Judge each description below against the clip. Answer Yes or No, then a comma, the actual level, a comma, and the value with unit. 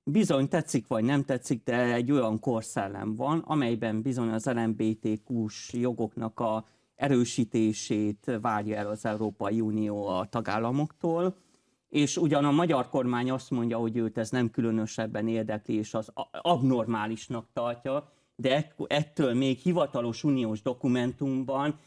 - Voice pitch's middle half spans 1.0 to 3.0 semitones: No, average, 3.6 semitones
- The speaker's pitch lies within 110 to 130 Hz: Yes, low, 120 Hz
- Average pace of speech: Yes, average, 130 wpm